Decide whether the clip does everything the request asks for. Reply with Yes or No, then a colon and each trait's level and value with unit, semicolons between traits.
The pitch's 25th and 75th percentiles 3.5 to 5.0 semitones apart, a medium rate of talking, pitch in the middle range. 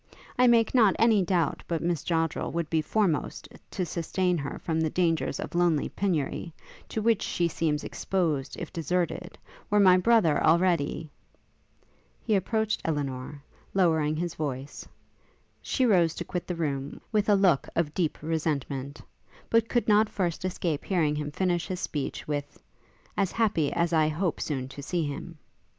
Yes: average, 3.9 semitones; average, 165 wpm; medium, 170 Hz